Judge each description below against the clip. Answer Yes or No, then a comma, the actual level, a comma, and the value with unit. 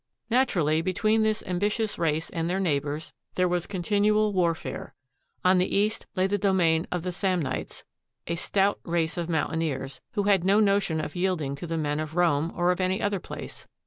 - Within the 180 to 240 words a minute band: Yes, average, 185 wpm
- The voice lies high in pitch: No, medium, 180 Hz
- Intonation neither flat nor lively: Yes, average, 3.5 semitones